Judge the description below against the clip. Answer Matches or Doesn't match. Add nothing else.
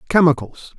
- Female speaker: Doesn't match